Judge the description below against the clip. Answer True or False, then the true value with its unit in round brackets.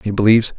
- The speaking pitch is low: True (110 Hz)